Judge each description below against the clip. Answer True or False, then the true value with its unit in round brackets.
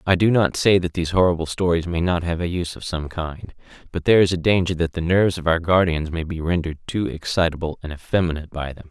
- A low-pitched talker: True (85 Hz)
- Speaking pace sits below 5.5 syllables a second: False (6.5 syllables/s)